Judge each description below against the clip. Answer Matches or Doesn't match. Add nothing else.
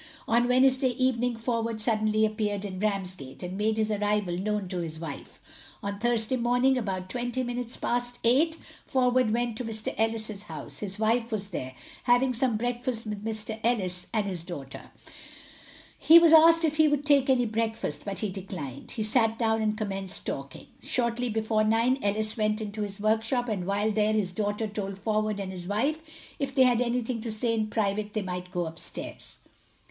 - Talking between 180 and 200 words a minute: Matches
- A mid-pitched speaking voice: Doesn't match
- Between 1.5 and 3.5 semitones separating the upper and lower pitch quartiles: Matches